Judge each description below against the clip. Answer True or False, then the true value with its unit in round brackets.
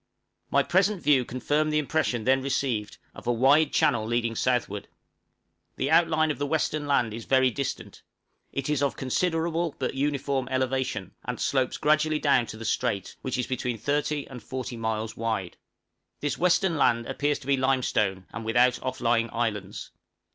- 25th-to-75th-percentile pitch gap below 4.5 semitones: True (3.9 semitones)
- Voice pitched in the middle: False (130 Hz)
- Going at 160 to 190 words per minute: True (170 wpm)